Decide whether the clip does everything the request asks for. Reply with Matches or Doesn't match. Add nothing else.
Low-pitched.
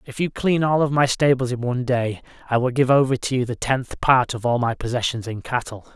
Matches